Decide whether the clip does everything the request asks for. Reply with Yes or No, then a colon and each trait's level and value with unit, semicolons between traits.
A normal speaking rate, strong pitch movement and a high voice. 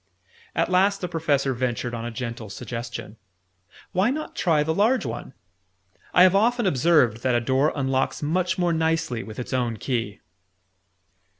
No: average, 160 wpm; wide, 6.8 semitones; medium, 140 Hz